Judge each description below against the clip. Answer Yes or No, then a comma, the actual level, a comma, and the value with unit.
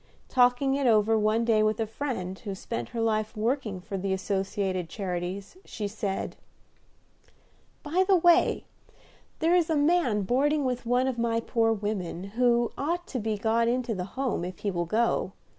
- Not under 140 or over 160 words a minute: No, average, 175 wpm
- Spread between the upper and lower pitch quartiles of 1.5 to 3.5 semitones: No, average, 4.3 semitones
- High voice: Yes, high, 225 Hz